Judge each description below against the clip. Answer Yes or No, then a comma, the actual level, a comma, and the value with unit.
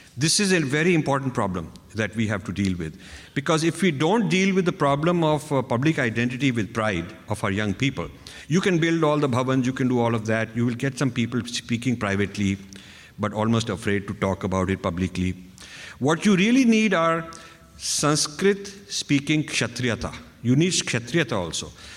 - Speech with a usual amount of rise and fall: No, wide, 7.8 semitones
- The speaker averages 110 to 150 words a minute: No, average, 190 wpm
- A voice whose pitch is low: Yes, low, 125 Hz